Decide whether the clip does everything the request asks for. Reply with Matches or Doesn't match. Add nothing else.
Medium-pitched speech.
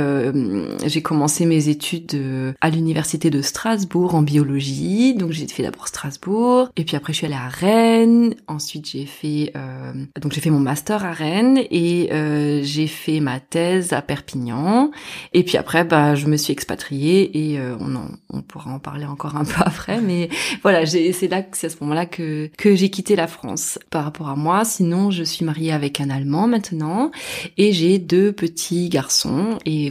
Matches